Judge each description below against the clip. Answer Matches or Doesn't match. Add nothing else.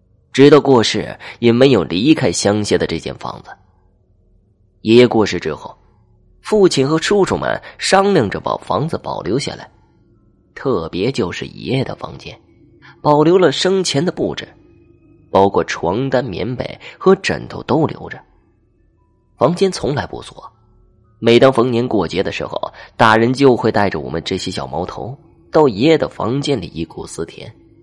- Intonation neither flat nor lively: Doesn't match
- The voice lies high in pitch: Doesn't match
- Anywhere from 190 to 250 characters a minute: Matches